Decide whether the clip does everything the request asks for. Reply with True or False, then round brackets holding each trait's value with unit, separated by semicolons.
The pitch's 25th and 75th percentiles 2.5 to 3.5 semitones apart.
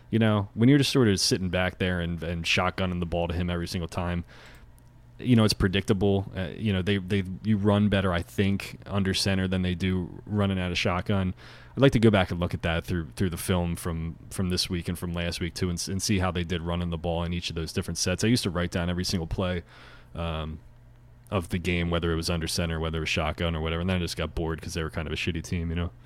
True (2.9 semitones)